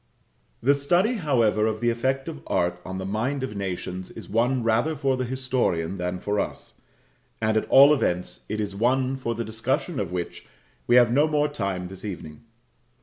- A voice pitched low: Yes, low, 115 Hz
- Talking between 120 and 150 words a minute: No, average, 185 wpm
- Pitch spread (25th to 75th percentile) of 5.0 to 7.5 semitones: Yes, wide, 5.4 semitones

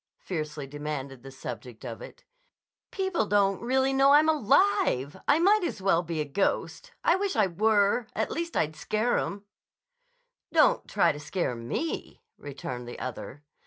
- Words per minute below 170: Yes, average, 160 wpm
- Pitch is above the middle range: Yes, high, 195 Hz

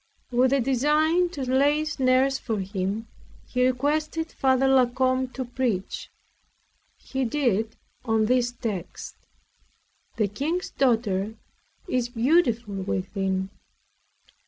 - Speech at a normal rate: No, slow, 110 wpm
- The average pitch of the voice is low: No, very high, 250 Hz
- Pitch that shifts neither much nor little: Yes, average, 3.6 semitones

